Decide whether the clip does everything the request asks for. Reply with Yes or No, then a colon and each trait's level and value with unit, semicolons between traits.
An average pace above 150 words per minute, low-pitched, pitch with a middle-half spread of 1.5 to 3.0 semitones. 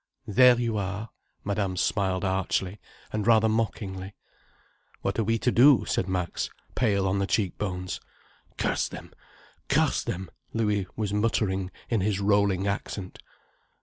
No: slow, 135 wpm; low, 100 Hz; narrow, 2.5 semitones